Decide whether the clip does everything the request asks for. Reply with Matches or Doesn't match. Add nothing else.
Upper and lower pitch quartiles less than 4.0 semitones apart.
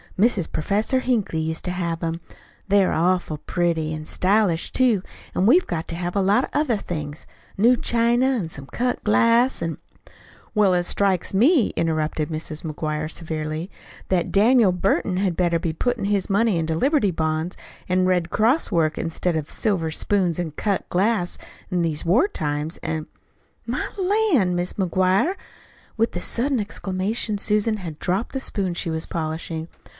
Doesn't match